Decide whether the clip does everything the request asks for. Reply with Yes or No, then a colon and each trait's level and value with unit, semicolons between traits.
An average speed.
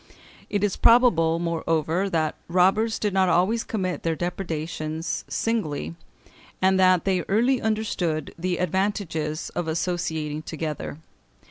No: slow, 120 wpm